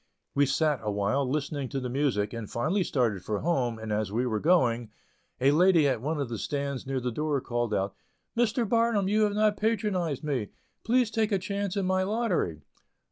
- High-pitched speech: No, medium, 140 Hz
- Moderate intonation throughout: No, wide, 8.2 semitones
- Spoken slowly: No, average, 195 wpm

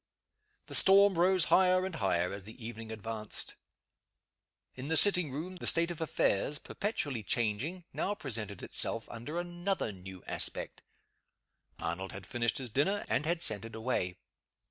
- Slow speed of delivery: No, average, 150 wpm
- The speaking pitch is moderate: No, low, 130 Hz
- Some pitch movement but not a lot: No, wide, 8.3 semitones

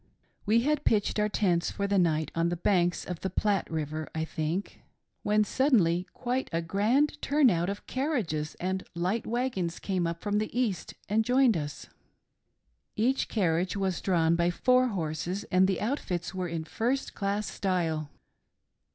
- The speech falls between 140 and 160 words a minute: No, average, 170 wpm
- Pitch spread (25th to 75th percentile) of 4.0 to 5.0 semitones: Yes, average, 4.7 semitones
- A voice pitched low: No, high, 190 Hz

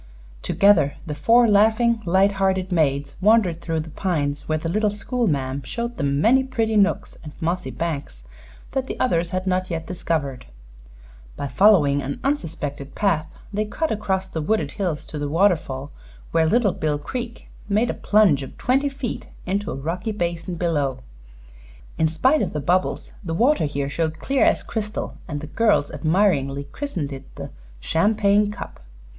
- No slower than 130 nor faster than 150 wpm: No, average, 165 wpm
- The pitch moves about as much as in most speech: No, wide, 6.1 semitones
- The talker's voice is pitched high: No, medium, 175 Hz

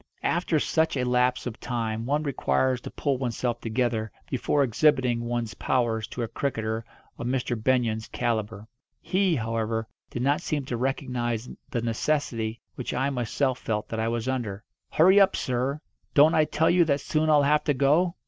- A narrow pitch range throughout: No, average, 3.8 semitones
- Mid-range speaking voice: No, low, 125 Hz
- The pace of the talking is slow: No, average, 175 wpm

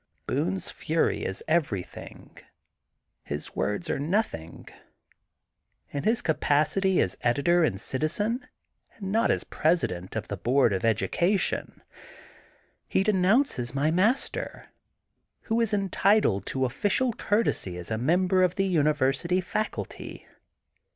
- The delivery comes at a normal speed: No, slow, 125 wpm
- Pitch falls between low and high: Yes, medium, 165 Hz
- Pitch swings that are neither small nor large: No, wide, 8.6 semitones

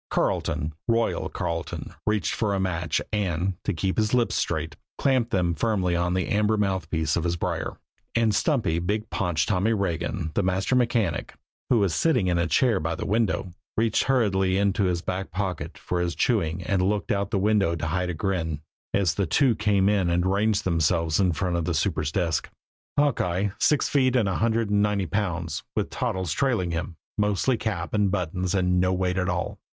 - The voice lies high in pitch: No, very low, 95 Hz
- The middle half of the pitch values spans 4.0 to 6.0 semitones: No, average, 3.5 semitones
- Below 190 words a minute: No, average, 195 wpm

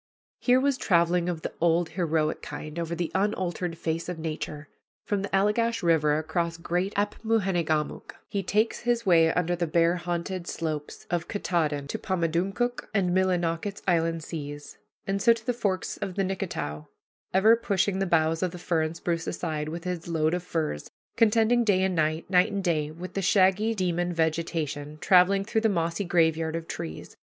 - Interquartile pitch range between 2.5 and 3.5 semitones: Yes, average, 3.2 semitones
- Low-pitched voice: No, medium, 175 Hz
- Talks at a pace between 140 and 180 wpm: Yes, average, 175 wpm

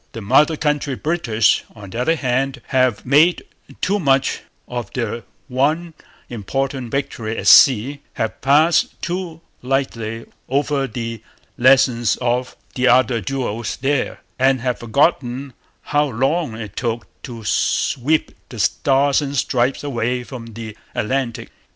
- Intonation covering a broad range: No, average, 3.3 semitones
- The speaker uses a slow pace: Yes, slow, 130 wpm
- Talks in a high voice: No, low, 130 Hz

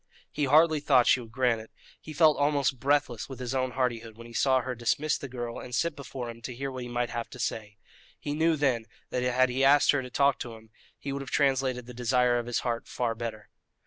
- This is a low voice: Yes, low, 125 Hz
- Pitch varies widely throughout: No, average, 2.8 semitones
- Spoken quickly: Yes, fast, 245 wpm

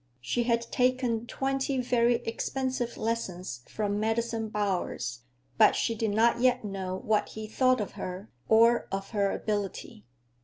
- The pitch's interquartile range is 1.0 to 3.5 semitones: Yes, average, 2.9 semitones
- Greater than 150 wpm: No, average, 145 wpm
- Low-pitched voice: No, high, 225 Hz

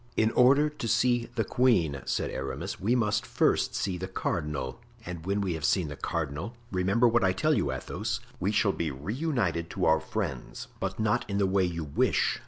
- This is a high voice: No, very low, 95 Hz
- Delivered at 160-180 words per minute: No, average, 190 wpm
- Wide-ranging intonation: Yes, wide, 6.2 semitones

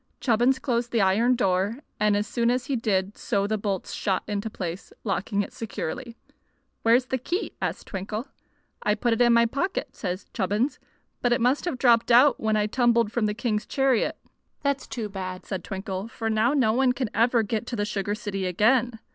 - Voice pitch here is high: Yes, high, 225 Hz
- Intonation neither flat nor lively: Yes, average, 3.1 semitones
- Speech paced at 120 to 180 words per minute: No, average, 195 wpm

